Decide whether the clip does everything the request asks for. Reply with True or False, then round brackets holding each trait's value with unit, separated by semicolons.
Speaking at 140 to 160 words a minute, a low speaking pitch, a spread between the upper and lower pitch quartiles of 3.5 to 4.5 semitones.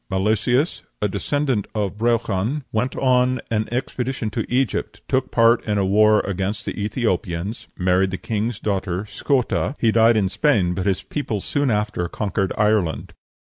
True (155 wpm; 110 Hz; 3.9 semitones)